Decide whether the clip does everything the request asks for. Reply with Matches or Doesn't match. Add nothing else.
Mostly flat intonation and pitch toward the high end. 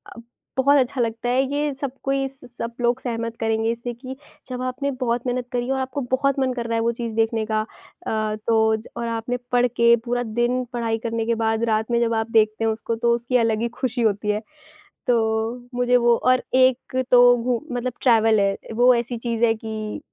Matches